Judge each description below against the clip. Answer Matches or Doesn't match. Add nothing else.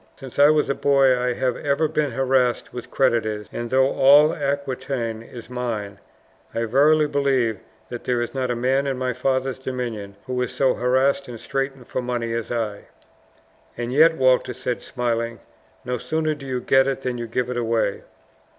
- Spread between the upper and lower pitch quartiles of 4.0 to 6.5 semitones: Doesn't match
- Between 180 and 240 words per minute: Matches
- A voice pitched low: Matches